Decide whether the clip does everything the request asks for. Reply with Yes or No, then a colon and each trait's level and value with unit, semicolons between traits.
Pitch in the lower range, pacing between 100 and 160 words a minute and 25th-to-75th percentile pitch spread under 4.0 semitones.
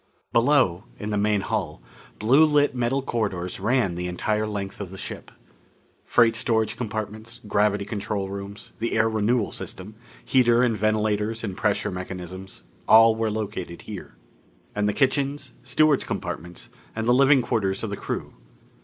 Yes: low, 110 Hz; average, 155 wpm; average, 3.0 semitones